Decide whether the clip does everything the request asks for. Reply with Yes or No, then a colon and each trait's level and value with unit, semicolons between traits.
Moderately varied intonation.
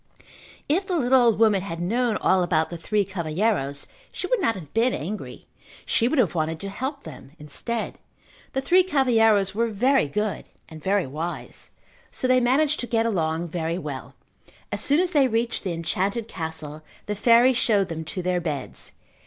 No: wide, 6.8 semitones